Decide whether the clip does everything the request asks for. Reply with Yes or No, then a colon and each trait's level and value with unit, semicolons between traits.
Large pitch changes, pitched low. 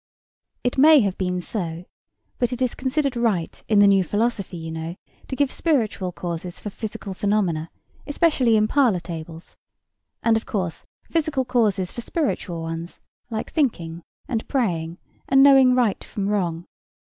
No: wide, 6.4 semitones; high, 210 Hz